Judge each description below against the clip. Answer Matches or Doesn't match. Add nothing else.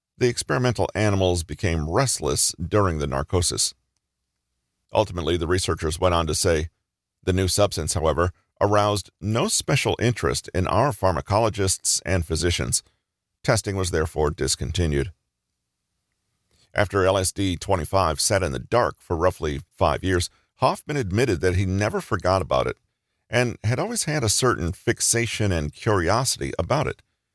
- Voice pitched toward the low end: Matches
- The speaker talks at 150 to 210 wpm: Doesn't match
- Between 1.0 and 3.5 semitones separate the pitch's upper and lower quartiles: Doesn't match